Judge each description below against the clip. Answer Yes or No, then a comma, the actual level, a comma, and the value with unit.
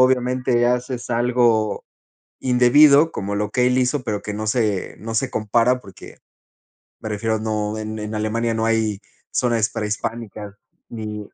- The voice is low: Yes, low, 115 Hz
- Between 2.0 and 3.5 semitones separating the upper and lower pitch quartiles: Yes, narrow, 2.6 semitones